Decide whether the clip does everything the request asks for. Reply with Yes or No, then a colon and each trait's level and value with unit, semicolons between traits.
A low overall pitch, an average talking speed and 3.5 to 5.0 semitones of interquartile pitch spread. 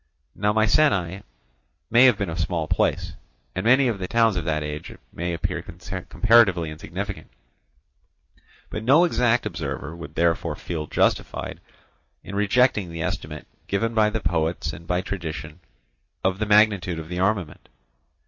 Yes: very low, 95 Hz; average, 150 wpm; average, 4.7 semitones